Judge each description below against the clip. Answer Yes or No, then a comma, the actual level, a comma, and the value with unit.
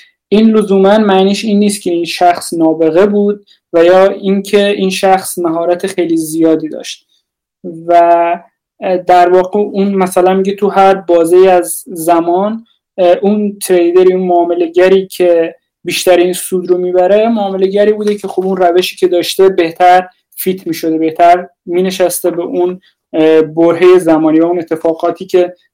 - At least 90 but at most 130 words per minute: No, average, 145 wpm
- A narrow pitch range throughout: Yes, narrow, 2.0 semitones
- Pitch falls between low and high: Yes, medium, 180 Hz